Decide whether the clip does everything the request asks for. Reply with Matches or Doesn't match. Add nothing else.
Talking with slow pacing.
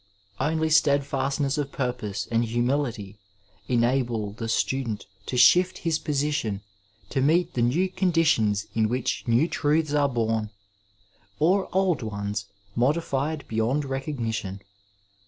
Matches